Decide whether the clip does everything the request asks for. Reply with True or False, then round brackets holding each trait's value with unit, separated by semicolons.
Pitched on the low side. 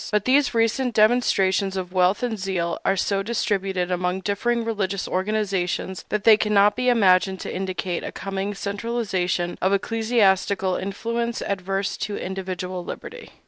False (195 Hz)